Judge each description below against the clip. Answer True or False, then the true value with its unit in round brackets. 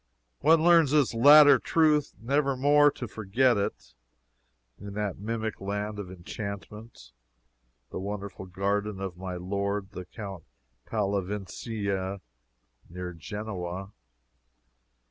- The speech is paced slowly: True (105 wpm)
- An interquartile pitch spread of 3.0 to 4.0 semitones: True (3.6 semitones)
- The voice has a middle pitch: False (105 Hz)